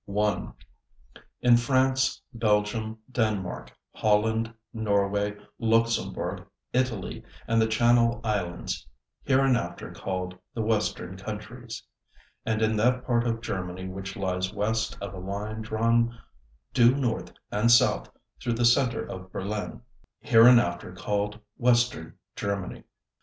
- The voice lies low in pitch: Yes, low, 110 Hz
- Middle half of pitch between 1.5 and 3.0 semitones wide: Yes, average, 2.7 semitones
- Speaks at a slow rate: Yes, slow, 115 wpm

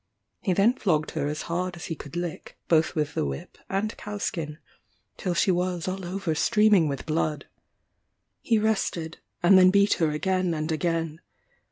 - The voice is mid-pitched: Yes, medium, 175 Hz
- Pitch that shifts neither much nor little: Yes, average, 3.5 semitones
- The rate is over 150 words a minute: Yes, average, 175 wpm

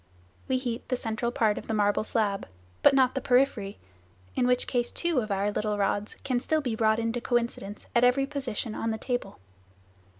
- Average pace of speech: Yes, average, 195 wpm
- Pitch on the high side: Yes, high, 235 Hz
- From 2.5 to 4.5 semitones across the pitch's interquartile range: Yes, average, 3.0 semitones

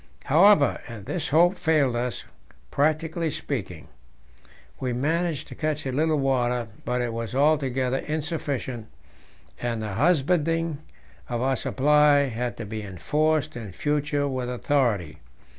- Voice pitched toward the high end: No, medium, 140 Hz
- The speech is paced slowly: Yes, slow, 125 wpm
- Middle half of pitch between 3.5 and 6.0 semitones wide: Yes, average, 4.2 semitones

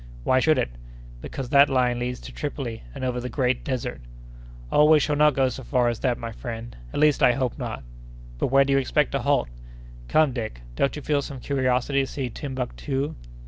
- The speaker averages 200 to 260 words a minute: Yes, fast, 205 wpm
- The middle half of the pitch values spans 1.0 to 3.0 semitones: Yes, narrow, 2.5 semitones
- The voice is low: Yes, low, 130 Hz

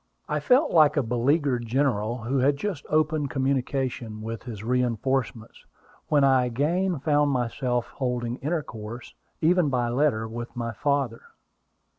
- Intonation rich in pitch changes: No, average, 3.6 semitones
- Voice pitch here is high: No, low, 130 Hz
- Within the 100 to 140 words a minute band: Yes, slow, 135 wpm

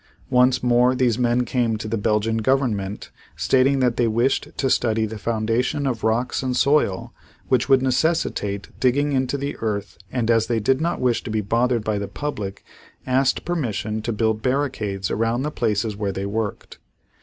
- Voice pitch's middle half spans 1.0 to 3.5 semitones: Yes, average, 3.1 semitones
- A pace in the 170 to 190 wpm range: Yes, average, 180 wpm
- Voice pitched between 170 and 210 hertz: No, low, 120 Hz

